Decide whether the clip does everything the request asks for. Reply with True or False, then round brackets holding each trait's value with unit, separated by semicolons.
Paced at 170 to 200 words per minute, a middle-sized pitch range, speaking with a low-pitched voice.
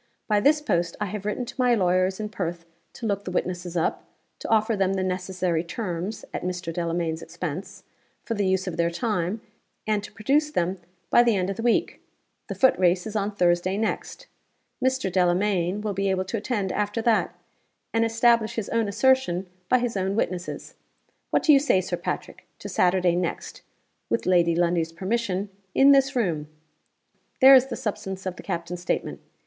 False (185 wpm; 4.2 semitones; 195 Hz)